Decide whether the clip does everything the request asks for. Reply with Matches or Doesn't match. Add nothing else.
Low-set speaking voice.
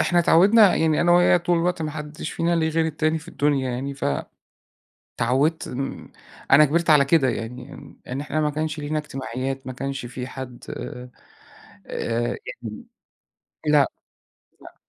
Doesn't match